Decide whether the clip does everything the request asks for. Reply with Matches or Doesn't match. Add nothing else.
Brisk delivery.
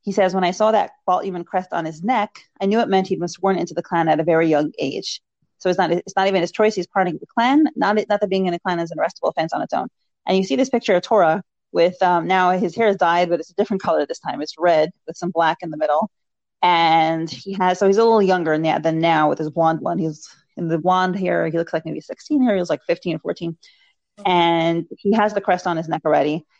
Matches